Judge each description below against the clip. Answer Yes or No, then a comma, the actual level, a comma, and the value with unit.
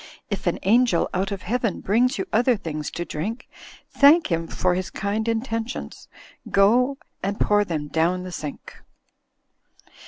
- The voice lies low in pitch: No, high, 200 Hz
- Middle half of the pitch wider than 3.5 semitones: Yes, average, 4.7 semitones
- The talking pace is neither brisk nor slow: Yes, average, 150 wpm